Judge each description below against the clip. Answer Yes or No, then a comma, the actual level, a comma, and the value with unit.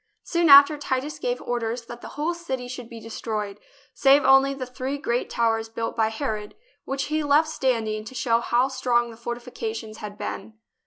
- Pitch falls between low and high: No, high, 245 Hz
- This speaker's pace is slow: No, average, 180 wpm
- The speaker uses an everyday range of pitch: Yes, average, 3.3 semitones